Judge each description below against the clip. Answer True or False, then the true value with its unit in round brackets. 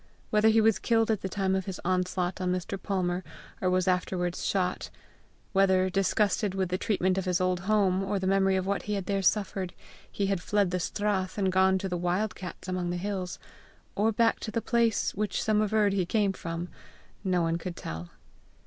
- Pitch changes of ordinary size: False (2.0 semitones)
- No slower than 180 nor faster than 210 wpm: True (205 wpm)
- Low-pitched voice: False (190 Hz)